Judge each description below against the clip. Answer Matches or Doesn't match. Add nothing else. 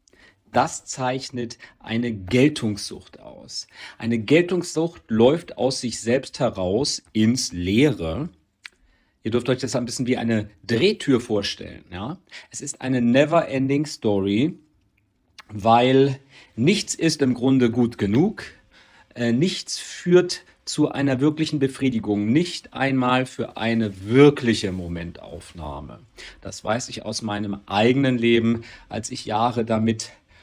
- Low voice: Matches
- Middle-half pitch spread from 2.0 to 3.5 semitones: Doesn't match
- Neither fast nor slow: Doesn't match